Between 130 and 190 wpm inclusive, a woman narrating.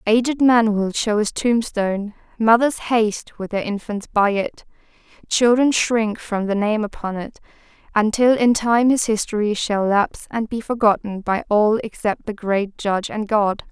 Yes: average, 165 wpm; female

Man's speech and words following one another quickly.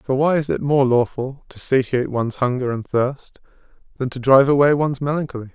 No: male; average, 195 wpm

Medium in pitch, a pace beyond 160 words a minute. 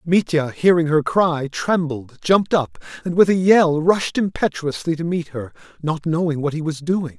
Yes: medium, 160 Hz; average, 185 wpm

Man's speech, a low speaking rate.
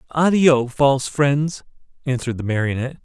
Yes: male; slow, 120 wpm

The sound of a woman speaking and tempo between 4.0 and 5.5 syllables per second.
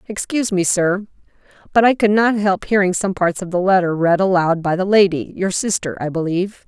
No: female; 5.7 syllables/s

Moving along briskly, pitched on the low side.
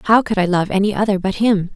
No: fast, 275 wpm; high, 200 Hz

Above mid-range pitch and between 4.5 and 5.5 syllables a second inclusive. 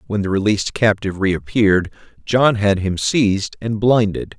No: low, 105 Hz; 5.0 syllables/s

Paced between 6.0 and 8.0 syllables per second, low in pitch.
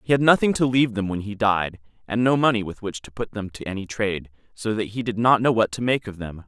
Yes: 6.1 syllables/s; low, 110 Hz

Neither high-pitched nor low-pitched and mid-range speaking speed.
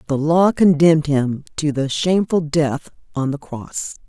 Yes: medium, 150 Hz; average, 160 wpm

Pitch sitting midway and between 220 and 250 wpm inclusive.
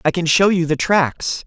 Yes: medium, 170 Hz; fast, 245 wpm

